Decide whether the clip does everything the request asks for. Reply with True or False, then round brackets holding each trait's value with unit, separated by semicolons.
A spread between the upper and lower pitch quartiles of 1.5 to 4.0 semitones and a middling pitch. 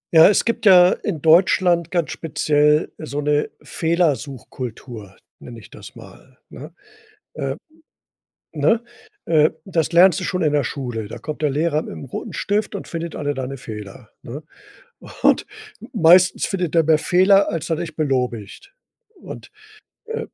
False (4.5 semitones; 155 Hz)